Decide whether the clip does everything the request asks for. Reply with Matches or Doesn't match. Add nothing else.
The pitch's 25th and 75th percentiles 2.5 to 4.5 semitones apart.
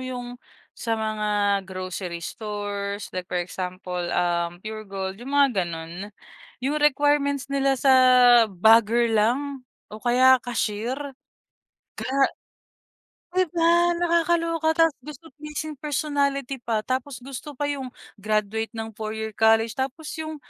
Doesn't match